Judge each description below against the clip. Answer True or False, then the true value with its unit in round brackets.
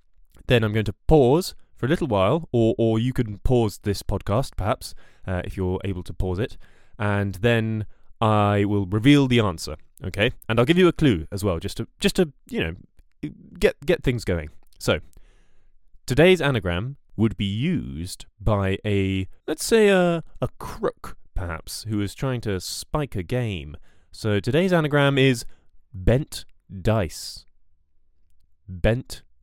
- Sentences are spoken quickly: False (160 wpm)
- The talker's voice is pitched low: True (105 Hz)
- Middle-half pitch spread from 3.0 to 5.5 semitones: True (4.9 semitones)